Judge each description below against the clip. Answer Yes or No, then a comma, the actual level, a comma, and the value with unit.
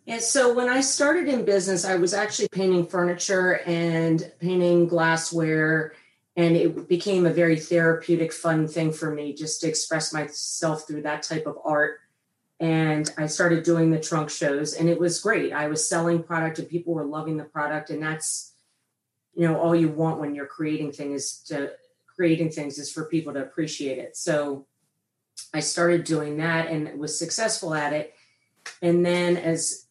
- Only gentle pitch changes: Yes, narrow, 2.0 semitones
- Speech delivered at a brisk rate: No, average, 175 wpm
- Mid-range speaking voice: Yes, medium, 160 Hz